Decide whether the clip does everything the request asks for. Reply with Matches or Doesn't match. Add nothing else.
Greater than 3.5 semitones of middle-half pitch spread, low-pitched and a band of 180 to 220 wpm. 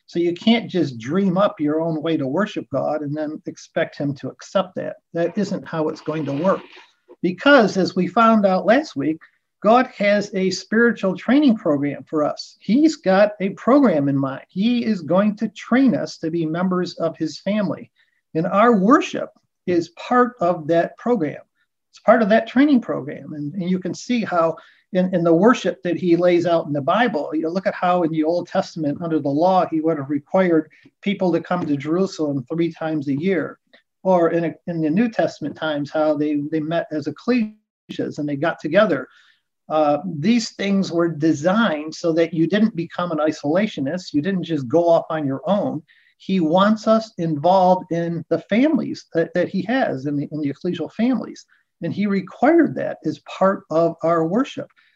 Doesn't match